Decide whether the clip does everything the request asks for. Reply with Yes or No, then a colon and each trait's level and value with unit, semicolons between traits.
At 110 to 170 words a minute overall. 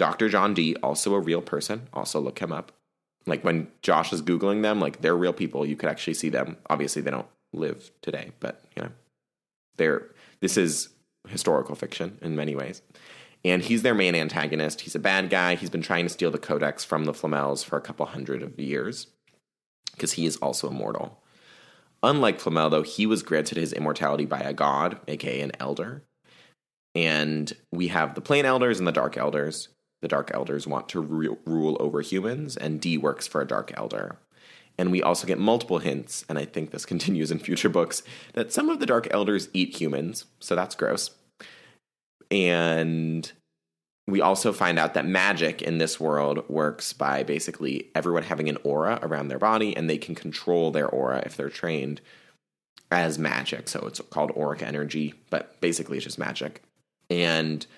No: average, 185 wpm